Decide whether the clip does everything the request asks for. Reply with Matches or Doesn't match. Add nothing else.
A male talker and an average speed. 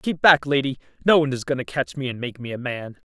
Doesn't match